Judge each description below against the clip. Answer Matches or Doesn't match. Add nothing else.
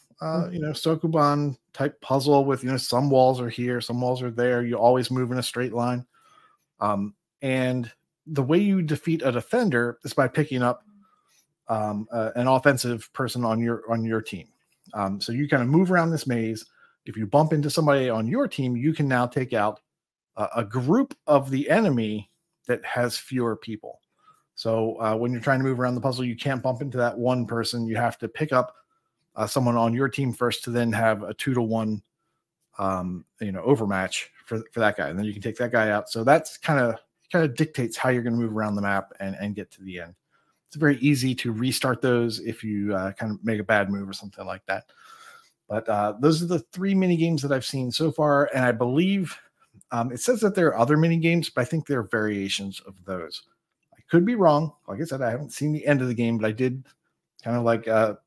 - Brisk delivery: Matches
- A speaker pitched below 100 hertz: Doesn't match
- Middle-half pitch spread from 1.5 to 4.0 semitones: Doesn't match